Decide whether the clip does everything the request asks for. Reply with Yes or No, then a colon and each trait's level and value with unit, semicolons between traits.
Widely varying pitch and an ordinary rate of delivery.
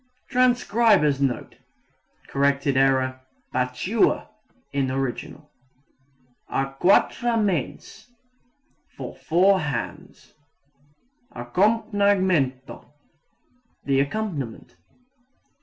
No: wide, 7.2 semitones; slow, 60 wpm